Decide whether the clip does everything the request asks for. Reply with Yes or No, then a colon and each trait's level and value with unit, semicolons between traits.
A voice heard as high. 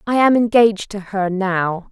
Yes: high, 205 Hz